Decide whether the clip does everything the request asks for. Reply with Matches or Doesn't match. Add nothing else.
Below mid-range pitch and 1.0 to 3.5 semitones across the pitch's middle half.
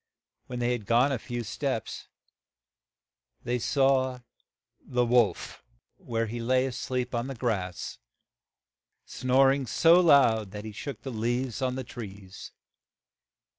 Matches